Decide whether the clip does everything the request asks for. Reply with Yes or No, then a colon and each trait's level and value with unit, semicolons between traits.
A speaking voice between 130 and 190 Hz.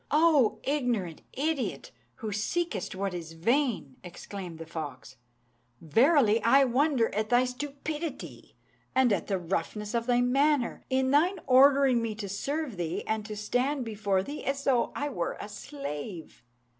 No: high, 240 Hz